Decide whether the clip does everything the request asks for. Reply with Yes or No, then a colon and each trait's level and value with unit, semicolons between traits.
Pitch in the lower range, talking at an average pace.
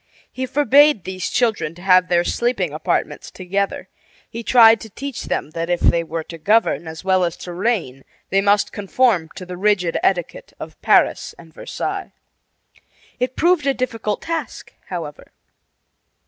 No: high, 195 Hz; average, 160 wpm